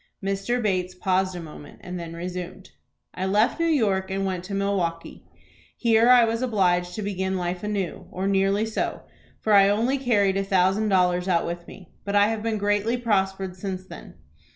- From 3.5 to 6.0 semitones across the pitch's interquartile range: No, narrow, 2.6 semitones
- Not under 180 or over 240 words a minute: Yes, average, 185 wpm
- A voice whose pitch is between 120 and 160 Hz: No, high, 195 Hz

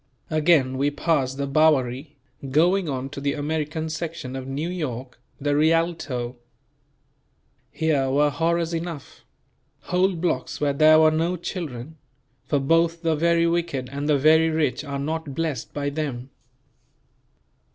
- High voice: No, medium, 155 Hz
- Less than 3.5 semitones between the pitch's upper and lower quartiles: Yes, average, 2.9 semitones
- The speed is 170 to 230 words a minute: No, average, 140 wpm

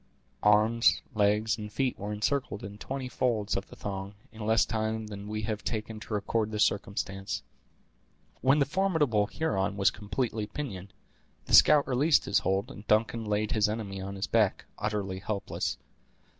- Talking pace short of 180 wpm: Yes, average, 165 wpm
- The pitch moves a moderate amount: No, narrow, 2.2 semitones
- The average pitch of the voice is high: No, low, 105 Hz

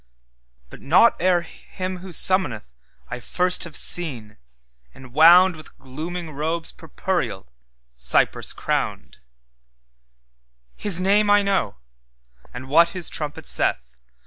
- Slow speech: Yes, slow, 95 wpm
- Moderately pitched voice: Yes, medium, 150 Hz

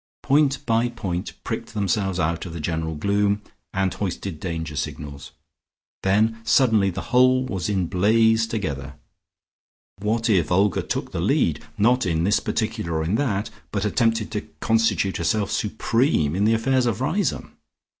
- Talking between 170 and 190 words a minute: No, average, 155 wpm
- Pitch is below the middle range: Yes, low, 105 Hz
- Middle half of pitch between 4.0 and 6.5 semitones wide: Yes, average, 4.3 semitones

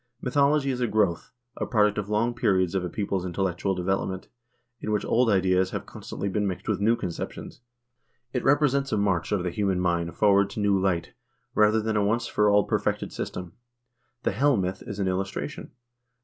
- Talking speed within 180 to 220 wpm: Yes, average, 190 wpm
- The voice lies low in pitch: Yes, low, 100 Hz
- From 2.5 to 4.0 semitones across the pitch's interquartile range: Yes, average, 3.0 semitones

